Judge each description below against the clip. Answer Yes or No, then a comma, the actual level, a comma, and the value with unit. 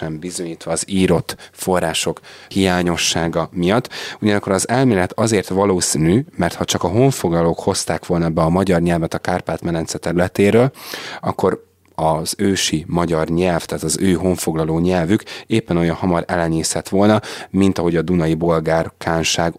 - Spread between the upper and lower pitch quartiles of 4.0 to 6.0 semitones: No, average, 2.8 semitones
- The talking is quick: No, average, 140 wpm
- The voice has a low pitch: Yes, very low, 90 Hz